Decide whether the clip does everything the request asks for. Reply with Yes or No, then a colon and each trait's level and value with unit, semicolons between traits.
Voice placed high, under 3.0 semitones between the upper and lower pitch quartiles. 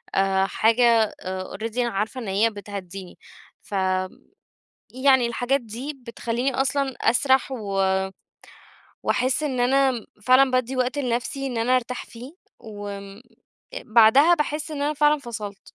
No: high, 240 Hz; average, 4.1 semitones